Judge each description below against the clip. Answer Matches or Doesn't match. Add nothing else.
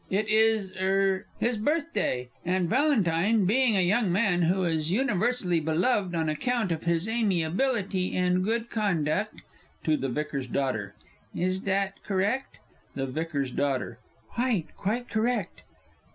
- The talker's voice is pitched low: Doesn't match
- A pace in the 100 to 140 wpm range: Matches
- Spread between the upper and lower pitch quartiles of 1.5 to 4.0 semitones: Doesn't match